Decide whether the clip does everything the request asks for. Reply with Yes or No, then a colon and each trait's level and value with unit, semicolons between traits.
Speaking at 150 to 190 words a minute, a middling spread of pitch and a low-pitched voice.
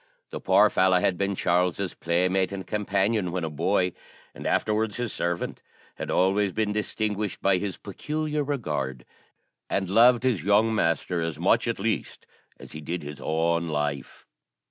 Yes: average, 160 wpm; average, 3.8 semitones; very low, 95 Hz